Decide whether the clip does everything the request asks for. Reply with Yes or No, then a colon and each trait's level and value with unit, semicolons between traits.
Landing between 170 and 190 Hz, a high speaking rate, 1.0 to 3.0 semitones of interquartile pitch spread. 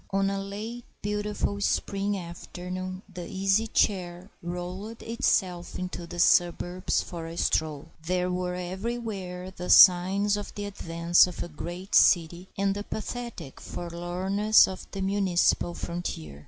No: medium, 185 Hz; slow, 135 wpm; narrow, 2.5 semitones